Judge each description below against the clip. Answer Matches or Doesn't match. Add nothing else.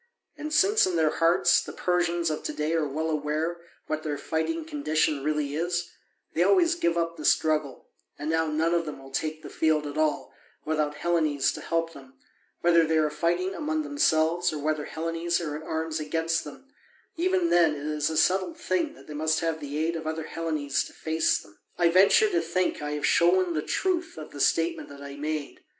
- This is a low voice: Doesn't match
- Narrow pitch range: Matches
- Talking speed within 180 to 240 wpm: Matches